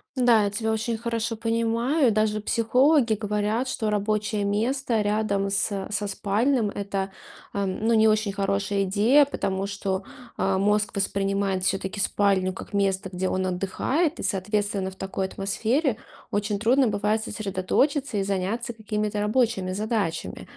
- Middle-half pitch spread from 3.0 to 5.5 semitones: No, narrow, 2.5 semitones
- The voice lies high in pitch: Yes, high, 210 Hz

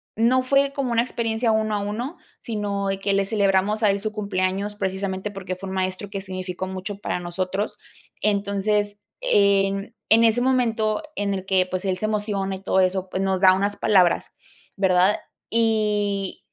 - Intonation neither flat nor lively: No, narrow, 2.2 semitones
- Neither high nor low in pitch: No, high, 200 Hz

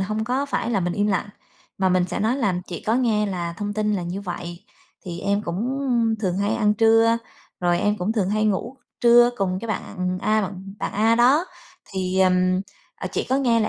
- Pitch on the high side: Yes, high, 210 Hz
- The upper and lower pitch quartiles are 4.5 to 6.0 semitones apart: No, average, 3.7 semitones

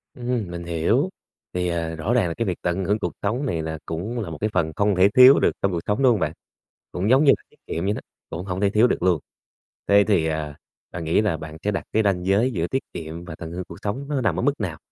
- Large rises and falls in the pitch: No, average, 4.7 semitones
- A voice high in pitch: No, very low, 95 Hz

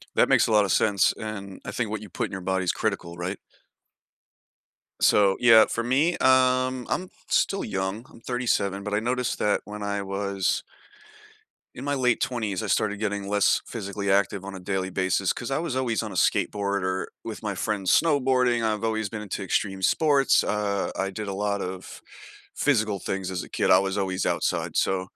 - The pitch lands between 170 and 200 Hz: No, low, 105 Hz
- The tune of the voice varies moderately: Yes, average, 3.3 semitones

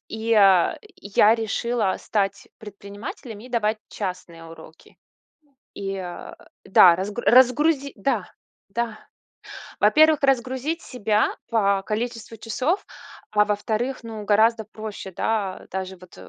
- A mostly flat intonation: No, average, 3.2 semitones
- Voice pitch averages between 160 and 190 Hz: No, high, 215 Hz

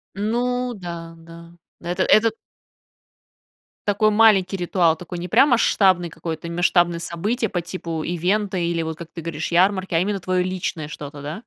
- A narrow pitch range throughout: No, average, 3.0 semitones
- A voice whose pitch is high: No, medium, 175 Hz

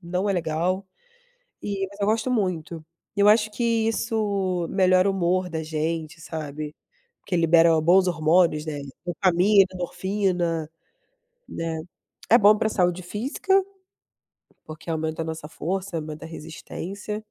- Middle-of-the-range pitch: Yes, medium, 180 Hz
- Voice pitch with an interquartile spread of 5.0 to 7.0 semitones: No, average, 3.7 semitones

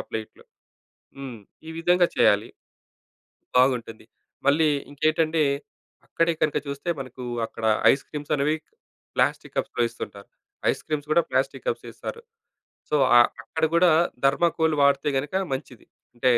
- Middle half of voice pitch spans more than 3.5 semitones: Yes, average, 4.0 semitones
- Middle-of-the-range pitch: Yes, medium, 145 Hz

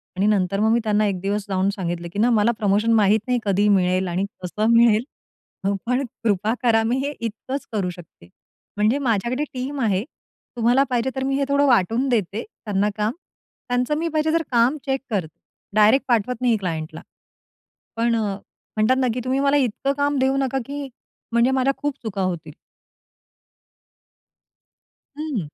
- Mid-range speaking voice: No, high, 225 Hz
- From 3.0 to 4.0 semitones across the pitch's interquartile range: No, average, 4.6 semitones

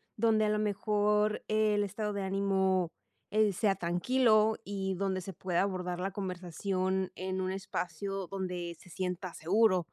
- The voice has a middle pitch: No, high, 195 Hz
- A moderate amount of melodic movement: No, narrow, 2.3 semitones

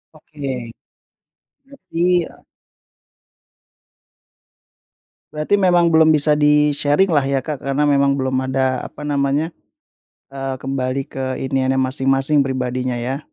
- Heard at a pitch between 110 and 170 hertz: Yes, medium, 140 Hz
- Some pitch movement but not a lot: No, narrow, 2.2 semitones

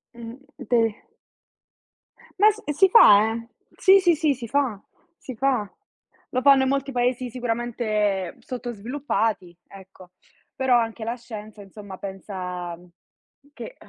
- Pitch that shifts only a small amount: No, average, 4.2 semitones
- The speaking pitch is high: Yes, high, 230 Hz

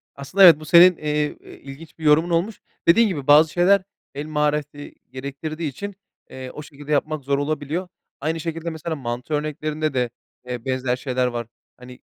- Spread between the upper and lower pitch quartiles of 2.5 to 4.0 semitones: Yes, average, 2.9 semitones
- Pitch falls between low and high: Yes, medium, 150 Hz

